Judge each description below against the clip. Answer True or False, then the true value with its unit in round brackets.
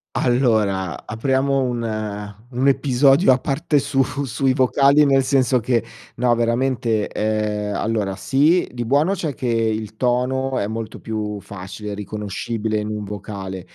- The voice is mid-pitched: False (120 Hz)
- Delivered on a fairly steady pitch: False (4.1 semitones)